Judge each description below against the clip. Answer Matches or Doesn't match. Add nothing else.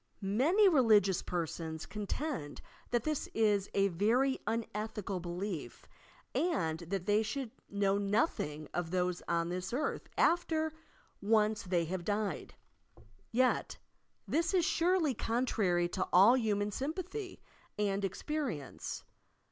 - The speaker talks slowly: Matches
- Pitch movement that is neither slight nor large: Doesn't match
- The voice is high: Matches